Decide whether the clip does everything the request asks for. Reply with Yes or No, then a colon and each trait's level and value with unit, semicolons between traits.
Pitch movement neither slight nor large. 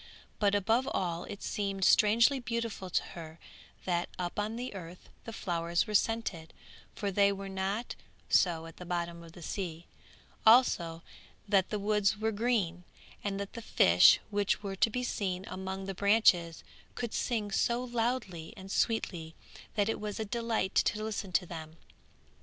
Yes: average, 3.8 semitones